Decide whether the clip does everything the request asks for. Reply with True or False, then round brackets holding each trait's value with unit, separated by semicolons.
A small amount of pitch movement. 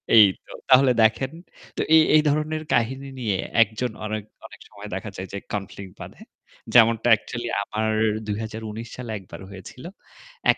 False (3.2 semitones)